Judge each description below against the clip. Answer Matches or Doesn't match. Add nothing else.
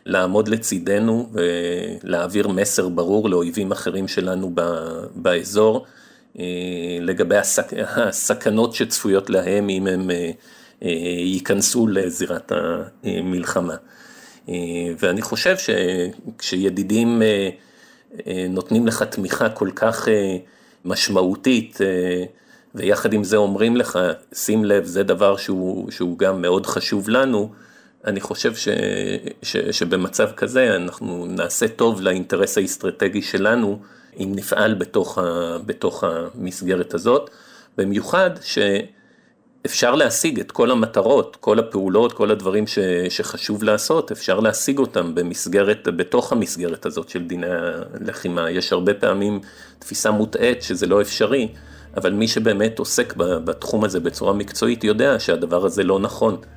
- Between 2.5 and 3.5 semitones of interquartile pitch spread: Matches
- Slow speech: Doesn't match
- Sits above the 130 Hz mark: Doesn't match